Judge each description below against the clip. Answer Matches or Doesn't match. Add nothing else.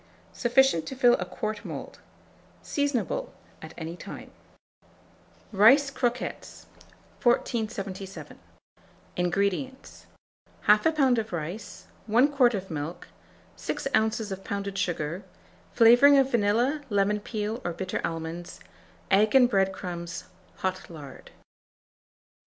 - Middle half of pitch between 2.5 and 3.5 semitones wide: Doesn't match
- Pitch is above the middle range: Matches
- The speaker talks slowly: Matches